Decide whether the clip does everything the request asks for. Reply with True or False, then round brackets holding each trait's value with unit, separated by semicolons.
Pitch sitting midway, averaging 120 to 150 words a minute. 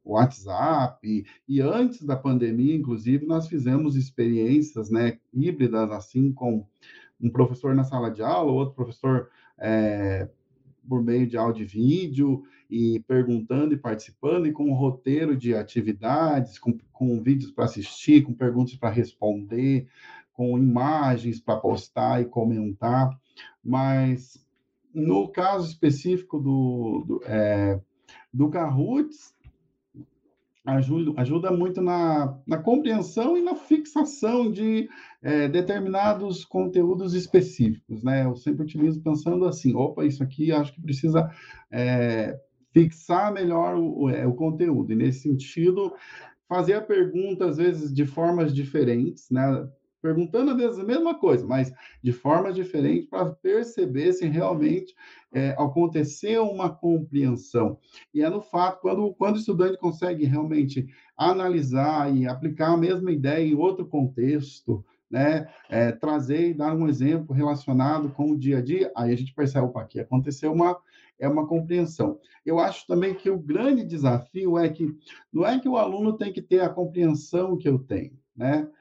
True (145 Hz; 145 wpm)